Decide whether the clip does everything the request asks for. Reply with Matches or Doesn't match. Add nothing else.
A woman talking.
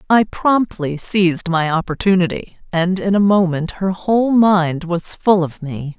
Matches